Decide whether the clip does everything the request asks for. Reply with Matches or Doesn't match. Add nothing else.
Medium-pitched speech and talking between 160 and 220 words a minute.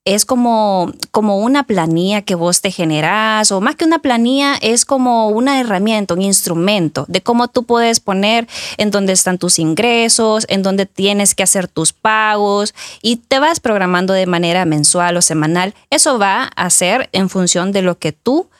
Doesn't match